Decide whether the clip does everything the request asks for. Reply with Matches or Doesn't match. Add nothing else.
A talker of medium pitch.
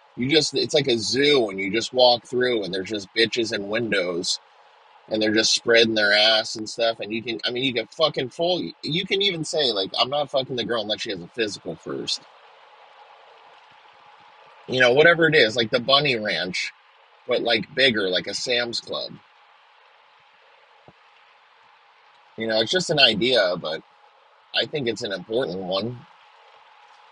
Doesn't match